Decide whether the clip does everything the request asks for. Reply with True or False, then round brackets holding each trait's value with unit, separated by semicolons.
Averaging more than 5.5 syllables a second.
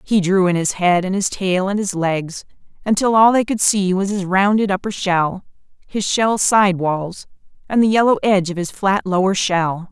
False (4.7 syllables/s)